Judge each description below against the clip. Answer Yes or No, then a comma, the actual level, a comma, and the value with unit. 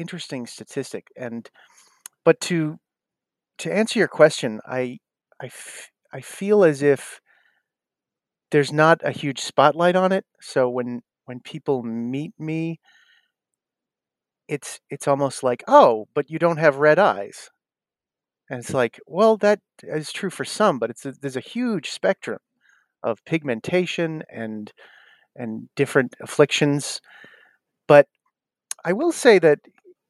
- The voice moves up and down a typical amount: No, wide, 5.9 semitones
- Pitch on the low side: No, medium, 150 Hz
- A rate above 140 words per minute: No, slow, 135 wpm